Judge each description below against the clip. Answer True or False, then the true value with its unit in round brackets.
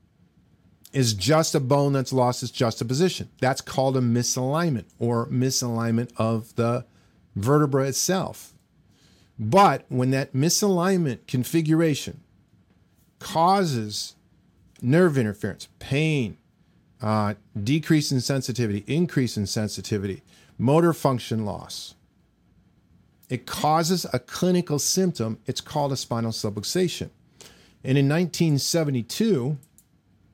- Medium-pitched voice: False (130 Hz)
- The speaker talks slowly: True (105 wpm)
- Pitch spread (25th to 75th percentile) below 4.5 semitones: False (5.5 semitones)